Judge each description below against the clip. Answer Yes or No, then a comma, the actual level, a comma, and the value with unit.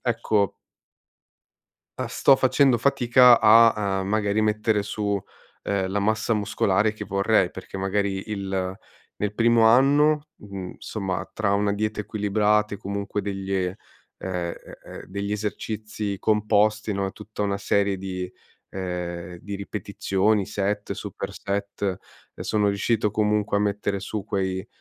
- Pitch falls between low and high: No, low, 100 Hz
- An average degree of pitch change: No, narrow, 1.7 semitones